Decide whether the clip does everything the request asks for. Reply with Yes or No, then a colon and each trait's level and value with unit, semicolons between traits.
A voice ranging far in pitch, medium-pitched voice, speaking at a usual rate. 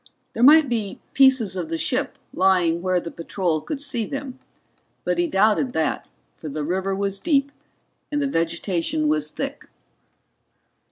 No: wide, 8.0 semitones; high, 195 Hz; average, 155 wpm